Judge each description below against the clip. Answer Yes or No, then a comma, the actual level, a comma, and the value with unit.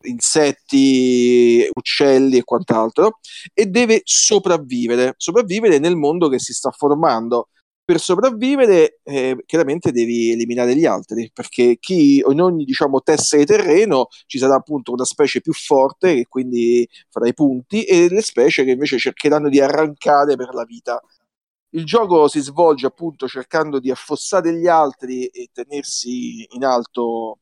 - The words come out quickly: No, average, 145 wpm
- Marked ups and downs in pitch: Yes, wide, 6.3 semitones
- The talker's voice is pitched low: No, medium, 145 Hz